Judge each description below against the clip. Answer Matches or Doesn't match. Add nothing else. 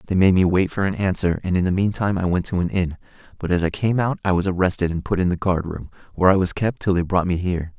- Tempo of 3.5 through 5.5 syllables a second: Doesn't match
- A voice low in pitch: Matches